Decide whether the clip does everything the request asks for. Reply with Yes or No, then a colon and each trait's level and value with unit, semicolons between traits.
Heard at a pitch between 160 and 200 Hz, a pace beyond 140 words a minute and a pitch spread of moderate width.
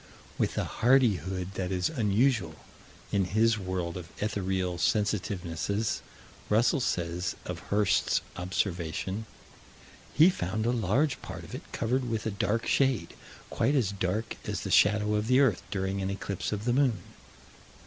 No: low, 105 Hz; average, 150 wpm; average, 3.7 semitones